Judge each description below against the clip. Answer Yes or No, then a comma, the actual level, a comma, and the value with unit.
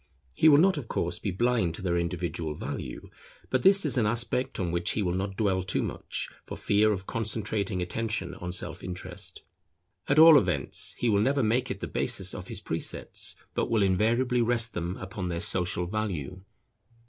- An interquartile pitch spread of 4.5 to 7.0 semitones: Yes, average, 4.8 semitones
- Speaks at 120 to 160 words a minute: No, average, 190 wpm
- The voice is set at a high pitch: No, low, 105 Hz